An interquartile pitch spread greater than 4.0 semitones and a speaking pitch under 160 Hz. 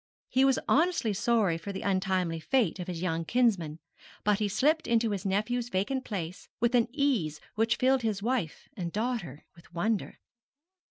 No: average, 5.3 semitones; high, 210 Hz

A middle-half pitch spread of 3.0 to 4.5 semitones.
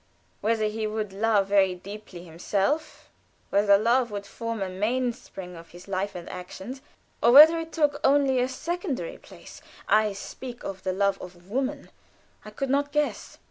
No: average, 5.2 semitones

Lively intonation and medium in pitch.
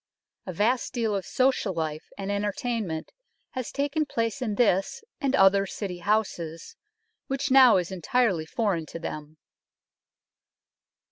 No: wide, 5.8 semitones; high, 205 Hz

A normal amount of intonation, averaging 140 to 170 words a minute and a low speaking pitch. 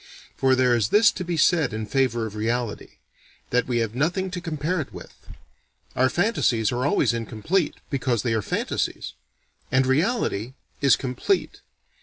No: wide, 5.9 semitones; average, 160 wpm; low, 130 Hz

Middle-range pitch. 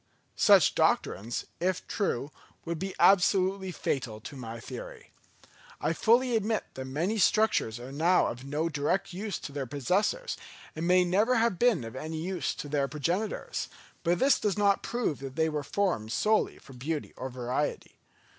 Yes: medium, 170 Hz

